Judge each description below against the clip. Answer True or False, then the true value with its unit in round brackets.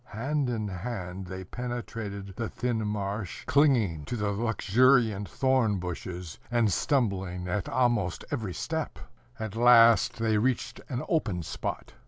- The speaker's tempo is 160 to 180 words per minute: False (135 wpm)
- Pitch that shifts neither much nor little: True (4.0 semitones)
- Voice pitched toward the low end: True (110 Hz)